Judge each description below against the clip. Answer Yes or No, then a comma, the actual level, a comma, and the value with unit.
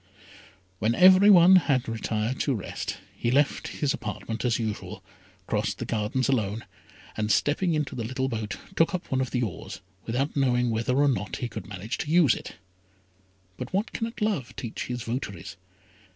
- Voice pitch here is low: Yes, low, 125 Hz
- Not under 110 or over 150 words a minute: No, average, 175 wpm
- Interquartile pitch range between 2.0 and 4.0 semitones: No, average, 4.6 semitones